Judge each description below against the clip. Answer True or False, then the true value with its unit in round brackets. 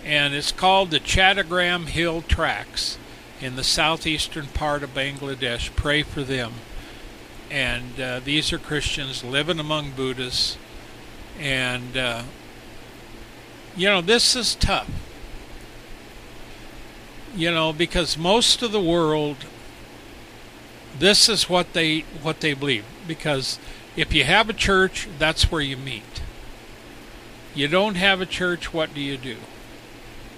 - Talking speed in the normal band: False (125 wpm)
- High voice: False (150 Hz)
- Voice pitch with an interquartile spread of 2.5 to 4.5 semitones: False (5.1 semitones)